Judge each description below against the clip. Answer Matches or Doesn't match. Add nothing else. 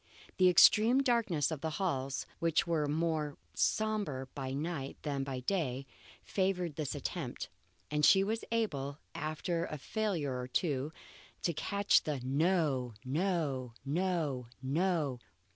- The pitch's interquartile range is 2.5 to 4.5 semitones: Doesn't match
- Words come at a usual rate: Doesn't match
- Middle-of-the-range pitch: Matches